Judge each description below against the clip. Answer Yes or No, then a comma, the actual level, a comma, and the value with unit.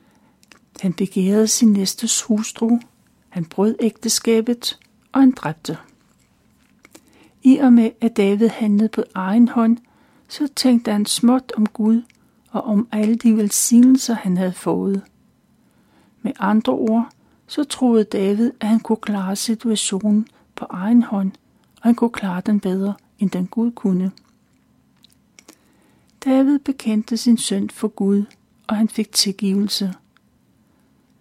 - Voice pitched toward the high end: Yes, high, 220 Hz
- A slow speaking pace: Yes, slow, 130 wpm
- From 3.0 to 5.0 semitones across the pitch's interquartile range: No, narrow, 2.6 semitones